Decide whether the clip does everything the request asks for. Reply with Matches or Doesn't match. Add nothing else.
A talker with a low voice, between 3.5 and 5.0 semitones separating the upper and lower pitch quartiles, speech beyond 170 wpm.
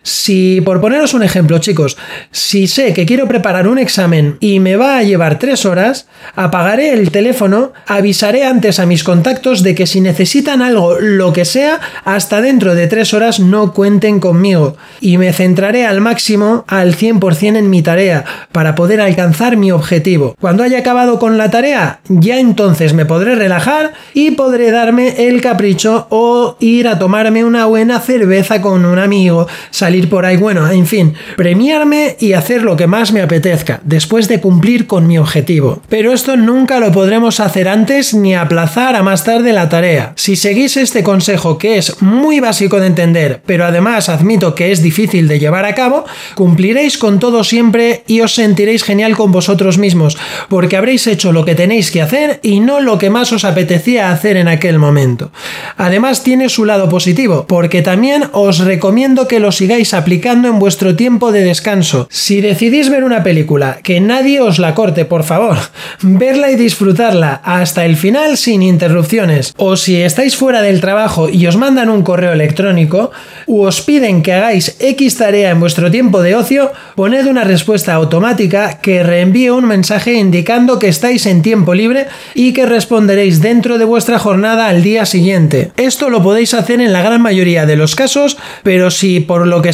Doesn't match